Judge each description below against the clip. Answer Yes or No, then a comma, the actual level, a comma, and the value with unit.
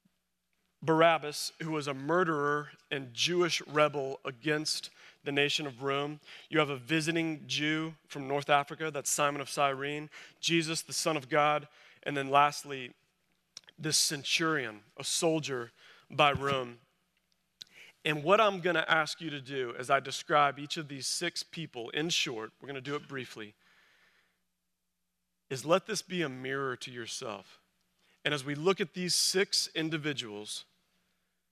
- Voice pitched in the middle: Yes, medium, 150 Hz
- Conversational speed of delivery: Yes, average, 150 wpm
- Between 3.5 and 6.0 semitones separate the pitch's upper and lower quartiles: No, average, 2.9 semitones